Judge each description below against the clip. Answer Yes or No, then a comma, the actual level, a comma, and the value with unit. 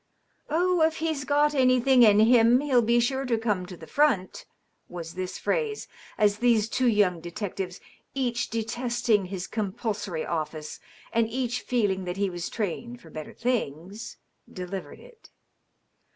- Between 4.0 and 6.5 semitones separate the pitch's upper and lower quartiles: Yes, average, 5.2 semitones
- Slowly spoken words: No, average, 150 wpm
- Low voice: No, high, 225 Hz